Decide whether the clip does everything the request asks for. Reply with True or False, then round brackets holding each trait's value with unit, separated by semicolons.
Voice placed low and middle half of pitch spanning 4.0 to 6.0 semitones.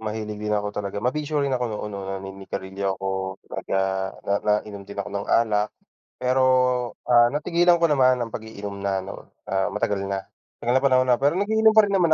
True (105 Hz; 4.8 semitones)